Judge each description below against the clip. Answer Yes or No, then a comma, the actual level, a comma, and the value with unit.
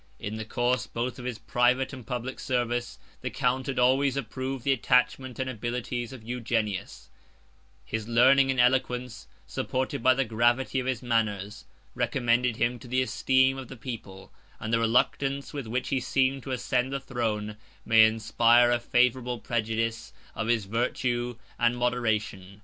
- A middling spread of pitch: No, narrow, 2.2 semitones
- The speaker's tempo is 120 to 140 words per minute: No, average, 160 wpm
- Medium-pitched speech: No, low, 120 Hz